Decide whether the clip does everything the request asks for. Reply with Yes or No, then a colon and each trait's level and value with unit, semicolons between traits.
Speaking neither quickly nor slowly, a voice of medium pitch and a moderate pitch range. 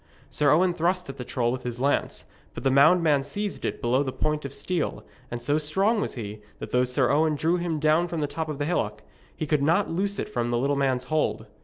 No: fast, 240 wpm; medium, 150 Hz; average, 4.3 semitones